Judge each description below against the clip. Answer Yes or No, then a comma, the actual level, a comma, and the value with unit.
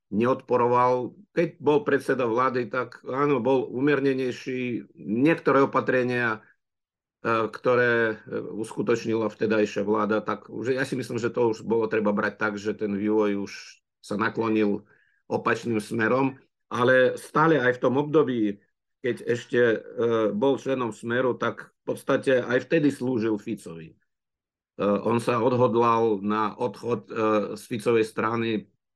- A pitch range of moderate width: Yes, average, 3.0 semitones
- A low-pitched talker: Yes, low, 120 Hz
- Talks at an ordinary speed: Yes, average, 125 wpm